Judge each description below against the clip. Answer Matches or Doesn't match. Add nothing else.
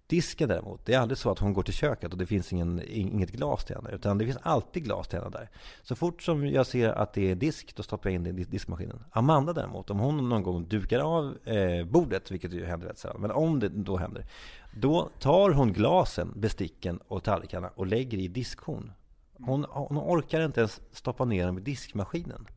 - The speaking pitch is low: Matches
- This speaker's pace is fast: Matches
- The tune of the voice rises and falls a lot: Matches